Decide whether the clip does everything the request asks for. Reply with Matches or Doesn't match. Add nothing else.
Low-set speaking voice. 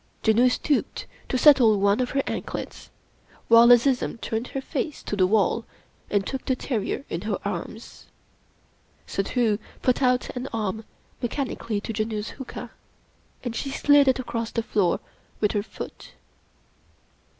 Doesn't match